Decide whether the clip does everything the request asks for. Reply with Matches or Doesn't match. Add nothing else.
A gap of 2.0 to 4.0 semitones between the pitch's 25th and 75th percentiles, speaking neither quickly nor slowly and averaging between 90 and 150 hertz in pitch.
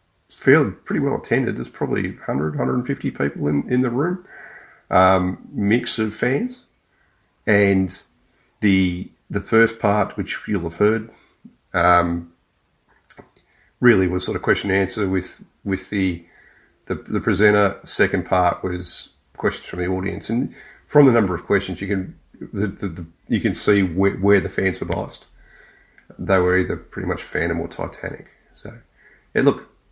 Matches